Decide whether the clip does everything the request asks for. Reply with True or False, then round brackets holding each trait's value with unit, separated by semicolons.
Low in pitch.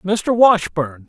False (185 Hz)